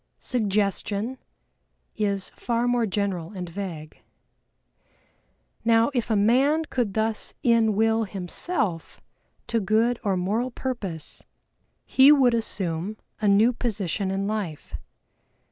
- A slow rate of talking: Yes, slow, 110 wpm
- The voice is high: Yes, high, 215 Hz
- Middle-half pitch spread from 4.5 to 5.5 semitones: No, average, 3.4 semitones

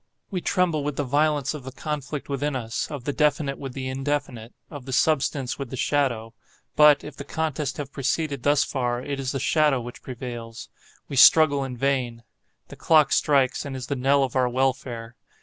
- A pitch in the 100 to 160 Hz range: Yes, low, 135 Hz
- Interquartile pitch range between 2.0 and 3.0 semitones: Yes, narrow, 2.6 semitones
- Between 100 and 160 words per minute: No, average, 185 wpm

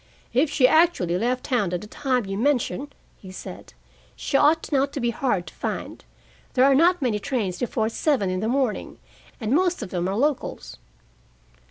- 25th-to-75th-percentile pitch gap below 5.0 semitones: No, wide, 5.4 semitones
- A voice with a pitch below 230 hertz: No, very high, 250 Hz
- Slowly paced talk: No, average, 185 wpm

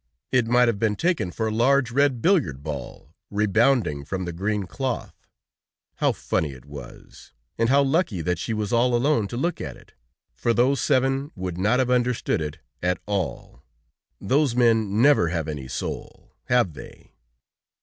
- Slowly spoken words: No, average, 170 wpm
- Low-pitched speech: Yes, low, 115 Hz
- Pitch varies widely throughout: Yes, wide, 5.8 semitones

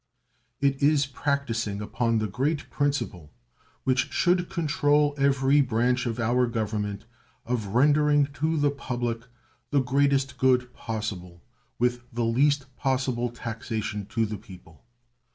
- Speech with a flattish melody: No, average, 3.8 semitones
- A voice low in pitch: Yes, low, 125 Hz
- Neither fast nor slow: No, slow, 125 wpm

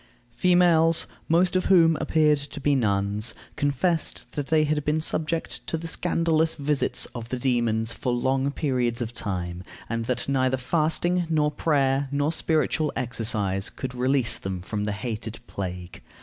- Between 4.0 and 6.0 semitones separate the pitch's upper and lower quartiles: Yes, wide, 5.4 semitones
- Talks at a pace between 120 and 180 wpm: Yes, average, 155 wpm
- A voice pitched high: No, low, 135 Hz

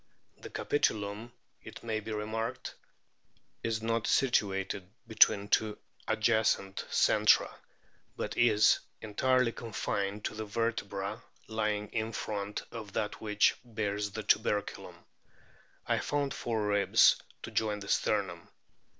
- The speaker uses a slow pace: Yes, slow, 115 wpm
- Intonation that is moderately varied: No, narrow, 1.7 semitones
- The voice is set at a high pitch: No, low, 105 Hz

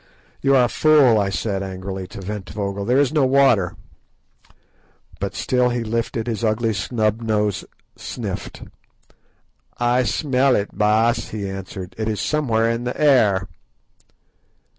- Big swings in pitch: No, average, 3.7 semitones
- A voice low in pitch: Yes, low, 110 Hz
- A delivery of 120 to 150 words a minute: Yes, average, 140 wpm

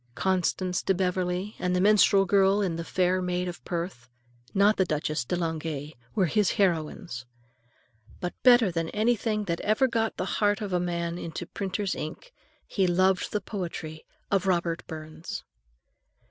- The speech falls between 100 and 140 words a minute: No, average, 160 wpm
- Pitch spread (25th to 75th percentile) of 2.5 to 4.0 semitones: Yes, average, 2.9 semitones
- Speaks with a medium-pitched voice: Yes, medium, 180 Hz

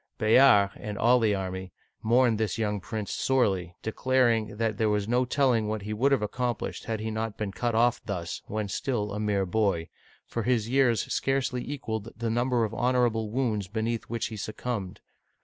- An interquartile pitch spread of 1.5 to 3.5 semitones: Yes, average, 2.7 semitones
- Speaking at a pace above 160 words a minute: Yes, average, 185 wpm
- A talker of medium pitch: No, low, 110 Hz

